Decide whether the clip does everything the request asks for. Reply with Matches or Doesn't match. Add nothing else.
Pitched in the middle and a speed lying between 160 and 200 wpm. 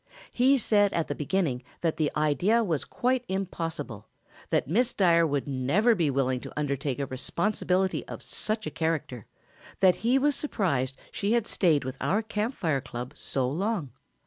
Matches